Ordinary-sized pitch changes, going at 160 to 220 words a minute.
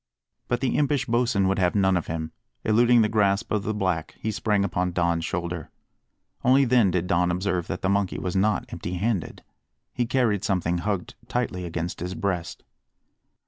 Yes: average, 3.6 semitones; average, 180 wpm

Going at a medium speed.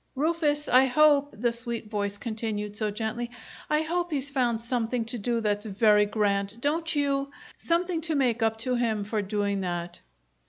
Yes: average, 170 wpm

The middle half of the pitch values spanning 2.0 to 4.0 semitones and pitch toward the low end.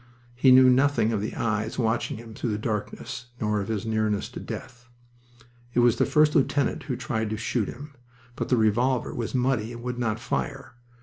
Yes: average, 2.7 semitones; low, 120 Hz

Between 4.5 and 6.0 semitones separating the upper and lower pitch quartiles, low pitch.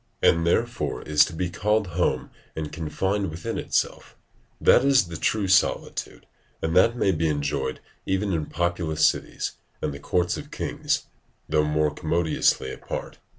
No: average, 3.7 semitones; very low, 85 Hz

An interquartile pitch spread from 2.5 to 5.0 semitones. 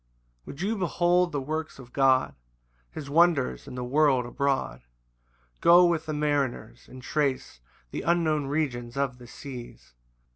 Yes: average, 3.8 semitones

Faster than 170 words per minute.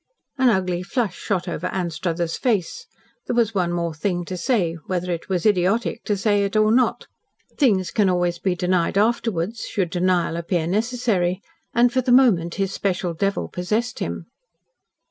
No: average, 165 wpm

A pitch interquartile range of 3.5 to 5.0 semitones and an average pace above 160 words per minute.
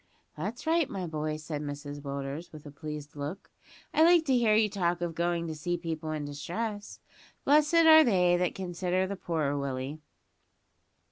No: wide, 5.4 semitones; average, 175 wpm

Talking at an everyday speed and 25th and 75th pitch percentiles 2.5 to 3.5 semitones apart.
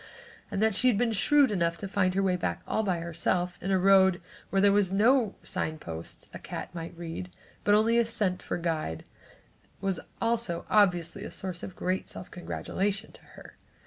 Yes: average, 190 wpm; average, 3.1 semitones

